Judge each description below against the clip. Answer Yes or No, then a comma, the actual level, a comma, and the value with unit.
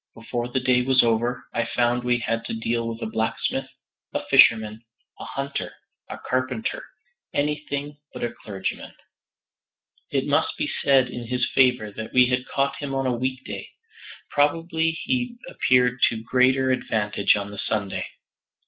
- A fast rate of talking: No, average, 155 wpm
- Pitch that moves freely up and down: No, average, 2.8 semitones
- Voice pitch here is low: Yes, low, 125 Hz